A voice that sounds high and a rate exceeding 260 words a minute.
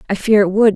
Yes: high, 205 Hz; fast, 320 wpm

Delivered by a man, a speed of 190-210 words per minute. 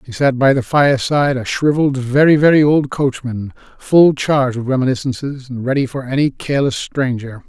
No: male; average, 170 wpm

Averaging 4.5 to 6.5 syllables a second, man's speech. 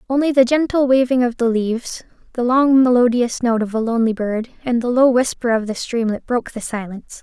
No: 5.7 syllables/s; female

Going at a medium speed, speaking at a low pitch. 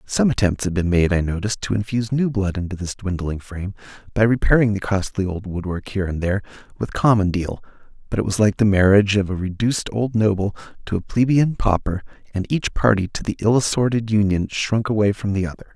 No: fast, 215 wpm; low, 100 Hz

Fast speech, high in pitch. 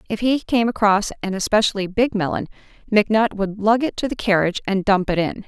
Yes: fast, 210 wpm; high, 210 Hz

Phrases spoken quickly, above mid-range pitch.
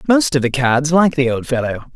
No: fast, 245 wpm; medium, 140 Hz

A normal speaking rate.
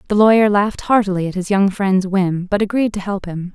No: fast, 235 wpm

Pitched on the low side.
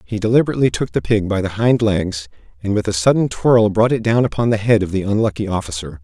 Yes: low, 105 Hz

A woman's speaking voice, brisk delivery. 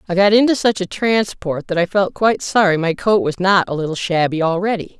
Yes: female; fast, 230 wpm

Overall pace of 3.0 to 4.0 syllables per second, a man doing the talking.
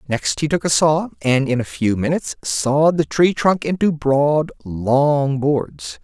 Yes: 3.9 syllables/s; male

